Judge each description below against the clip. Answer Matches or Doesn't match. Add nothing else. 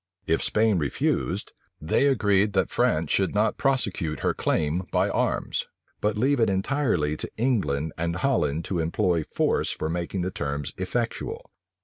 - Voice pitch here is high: Doesn't match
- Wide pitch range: Matches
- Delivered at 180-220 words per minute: Doesn't match